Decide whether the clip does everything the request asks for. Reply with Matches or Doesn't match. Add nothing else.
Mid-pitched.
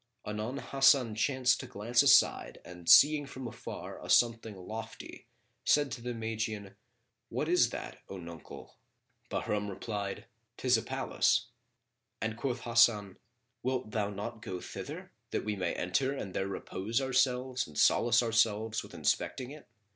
Doesn't match